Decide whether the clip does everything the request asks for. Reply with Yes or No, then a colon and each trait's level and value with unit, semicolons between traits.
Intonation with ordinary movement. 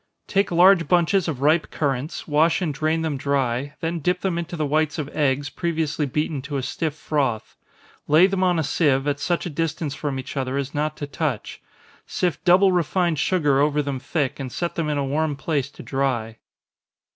Yes: average, 3.3 semitones